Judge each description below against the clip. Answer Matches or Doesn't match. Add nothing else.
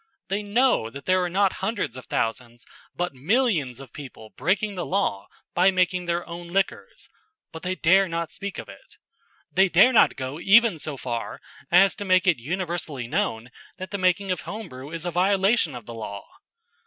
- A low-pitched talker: Doesn't match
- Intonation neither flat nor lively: Doesn't match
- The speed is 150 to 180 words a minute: Doesn't match